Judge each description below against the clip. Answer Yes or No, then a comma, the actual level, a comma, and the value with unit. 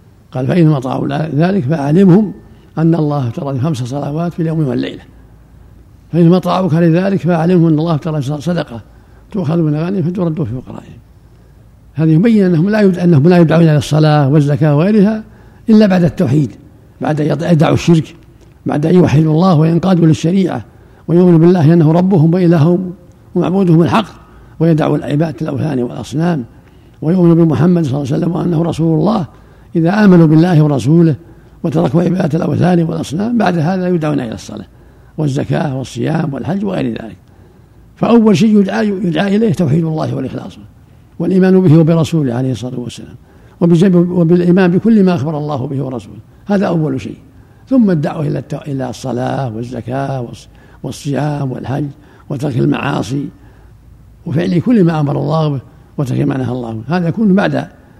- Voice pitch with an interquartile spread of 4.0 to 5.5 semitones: Yes, average, 4.3 semitones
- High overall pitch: No, medium, 160 Hz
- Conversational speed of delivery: No, fast, 140 wpm